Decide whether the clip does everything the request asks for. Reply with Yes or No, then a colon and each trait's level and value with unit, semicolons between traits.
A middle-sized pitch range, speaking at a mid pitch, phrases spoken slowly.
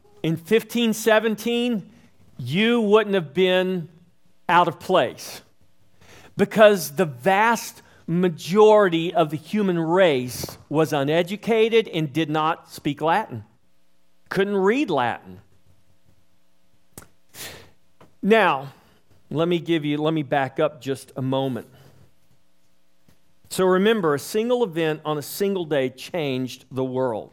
No: wide, 7.1 semitones; medium, 160 Hz; slow, 110 wpm